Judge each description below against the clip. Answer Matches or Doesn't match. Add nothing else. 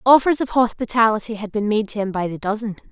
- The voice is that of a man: Doesn't match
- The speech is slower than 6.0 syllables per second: Doesn't match